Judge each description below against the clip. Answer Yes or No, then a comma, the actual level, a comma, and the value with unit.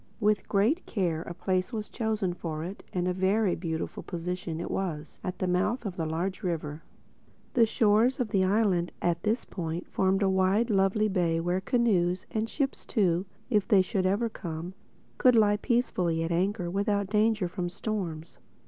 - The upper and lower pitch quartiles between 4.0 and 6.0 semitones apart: No, average, 3.4 semitones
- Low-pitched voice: No, high, 190 Hz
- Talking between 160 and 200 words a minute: Yes, average, 165 wpm